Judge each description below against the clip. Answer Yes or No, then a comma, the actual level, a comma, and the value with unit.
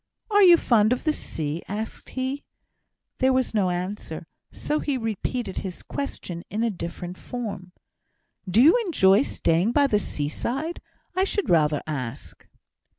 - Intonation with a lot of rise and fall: Yes, wide, 6.9 semitones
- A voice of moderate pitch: No, high, 220 Hz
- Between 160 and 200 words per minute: No, average, 150 wpm